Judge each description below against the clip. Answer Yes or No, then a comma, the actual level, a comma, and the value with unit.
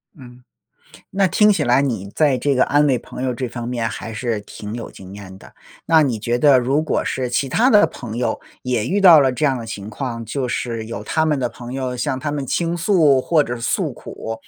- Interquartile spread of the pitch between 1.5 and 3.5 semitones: No, average, 4.1 semitones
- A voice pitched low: Yes, low, 130 Hz